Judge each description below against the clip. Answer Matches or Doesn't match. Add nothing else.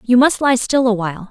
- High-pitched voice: Matches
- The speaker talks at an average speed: Doesn't match